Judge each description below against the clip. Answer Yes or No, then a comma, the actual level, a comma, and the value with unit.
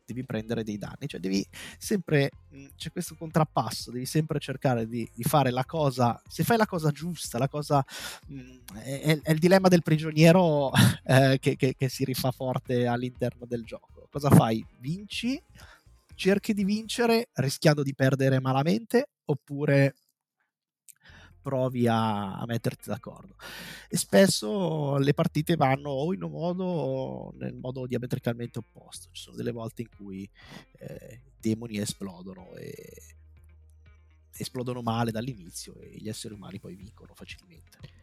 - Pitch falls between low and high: No, low, 130 Hz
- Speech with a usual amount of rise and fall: No, wide, 6.0 semitones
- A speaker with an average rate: Yes, average, 150 wpm